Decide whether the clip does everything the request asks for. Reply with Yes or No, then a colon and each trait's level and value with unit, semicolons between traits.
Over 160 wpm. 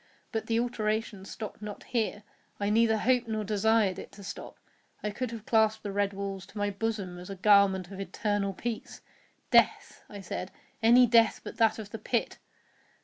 Yes: average, 180 wpm